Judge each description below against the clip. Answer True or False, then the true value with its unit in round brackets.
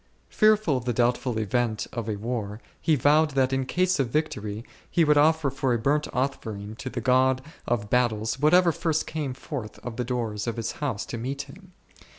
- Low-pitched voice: True (130 Hz)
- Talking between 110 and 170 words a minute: False (195 wpm)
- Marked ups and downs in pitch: False (4.5 semitones)